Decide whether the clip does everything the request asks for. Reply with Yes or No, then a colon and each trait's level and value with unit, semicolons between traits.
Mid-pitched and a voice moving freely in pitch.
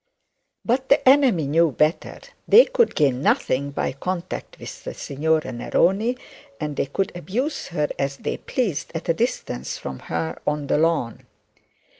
Yes: medium, 160 Hz; wide, 8.2 semitones